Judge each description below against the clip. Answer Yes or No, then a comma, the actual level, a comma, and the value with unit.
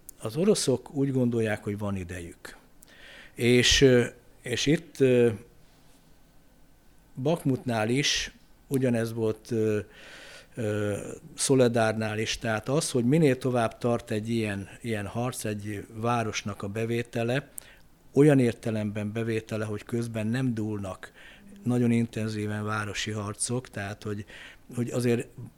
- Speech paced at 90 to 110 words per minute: Yes, slow, 105 wpm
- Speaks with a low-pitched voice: Yes, low, 115 Hz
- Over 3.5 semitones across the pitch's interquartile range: No, average, 2.9 semitones